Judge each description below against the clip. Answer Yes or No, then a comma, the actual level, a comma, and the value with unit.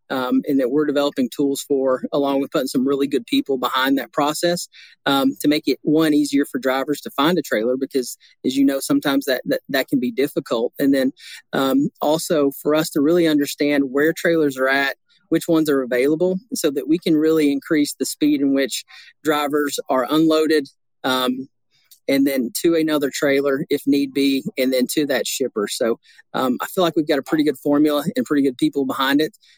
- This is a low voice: No, medium, 145 Hz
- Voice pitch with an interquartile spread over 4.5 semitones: No, average, 2.9 semitones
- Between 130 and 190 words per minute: No, fast, 205 wpm